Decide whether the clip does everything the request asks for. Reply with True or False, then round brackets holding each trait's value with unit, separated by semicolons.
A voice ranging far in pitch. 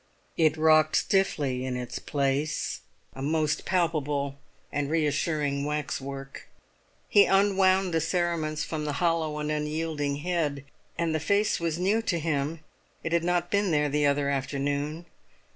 False (3.0 semitones)